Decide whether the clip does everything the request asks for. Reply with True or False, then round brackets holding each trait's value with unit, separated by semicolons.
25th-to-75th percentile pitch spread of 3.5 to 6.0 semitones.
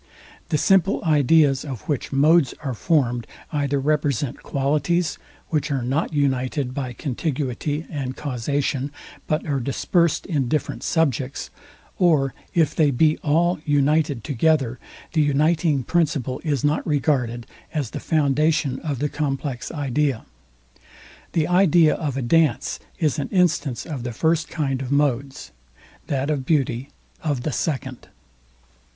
False (2.9 semitones)